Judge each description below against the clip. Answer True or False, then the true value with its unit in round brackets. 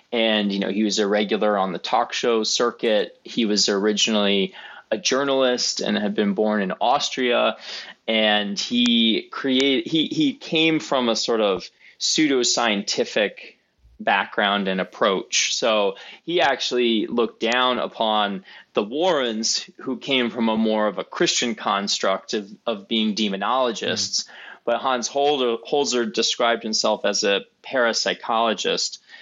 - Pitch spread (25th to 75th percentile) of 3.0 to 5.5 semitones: True (4.0 semitones)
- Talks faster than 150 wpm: False (140 wpm)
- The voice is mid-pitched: False (115 Hz)